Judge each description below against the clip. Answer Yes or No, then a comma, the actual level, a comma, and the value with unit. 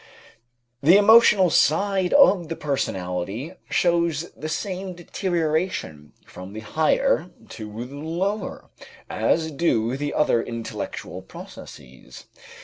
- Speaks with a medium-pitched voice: Yes, medium, 160 Hz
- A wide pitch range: Yes, wide, 7.8 semitones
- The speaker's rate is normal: No, slow, 105 wpm